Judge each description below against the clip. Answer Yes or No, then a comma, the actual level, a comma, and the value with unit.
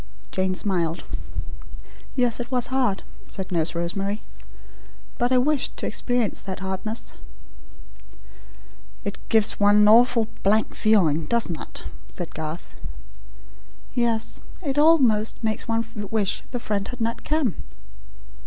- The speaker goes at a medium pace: No, slow, 125 wpm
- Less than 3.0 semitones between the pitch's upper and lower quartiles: No, average, 4.1 semitones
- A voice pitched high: Yes, high, 220 Hz